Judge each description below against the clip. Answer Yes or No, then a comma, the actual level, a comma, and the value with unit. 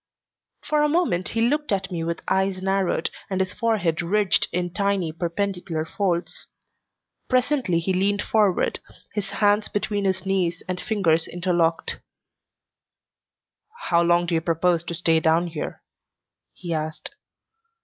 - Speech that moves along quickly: No, average, 140 wpm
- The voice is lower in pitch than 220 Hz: Yes, medium, 185 Hz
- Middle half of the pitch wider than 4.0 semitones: No, average, 3.2 semitones